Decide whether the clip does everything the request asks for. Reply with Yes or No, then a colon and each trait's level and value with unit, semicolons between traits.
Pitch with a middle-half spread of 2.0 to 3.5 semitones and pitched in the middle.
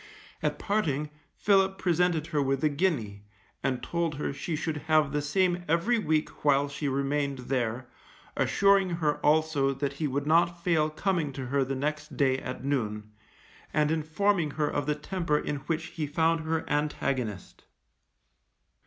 Yes: average, 3.2 semitones; medium, 150 Hz